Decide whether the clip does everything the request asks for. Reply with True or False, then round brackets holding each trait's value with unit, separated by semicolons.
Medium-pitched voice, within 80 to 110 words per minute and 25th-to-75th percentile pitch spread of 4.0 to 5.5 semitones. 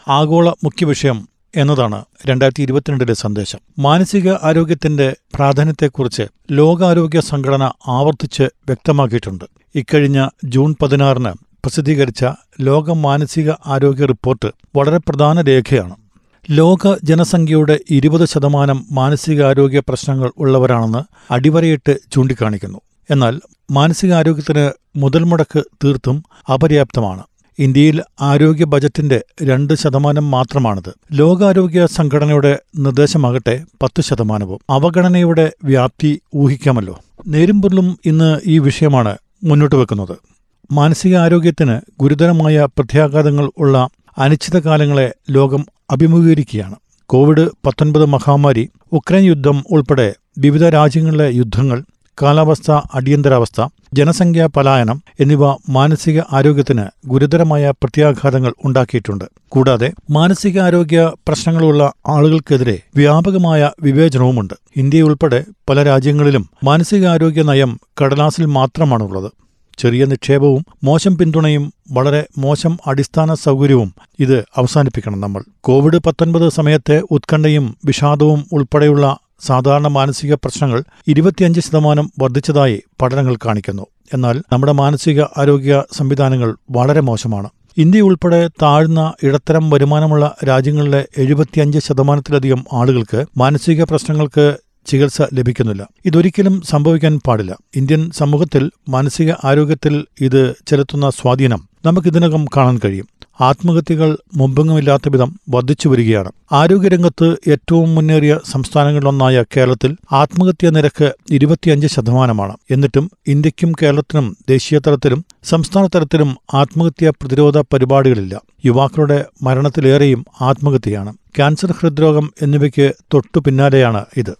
False (145 Hz; 90 wpm; 3.0 semitones)